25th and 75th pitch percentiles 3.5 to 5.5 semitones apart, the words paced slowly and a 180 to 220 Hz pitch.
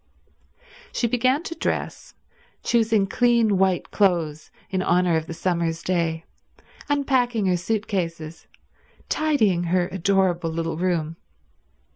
Yes: average, 5.0 semitones; slow, 115 wpm; medium, 185 Hz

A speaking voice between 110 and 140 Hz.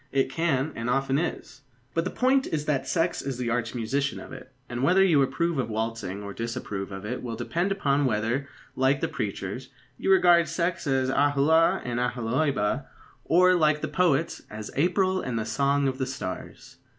Yes: low, 135 Hz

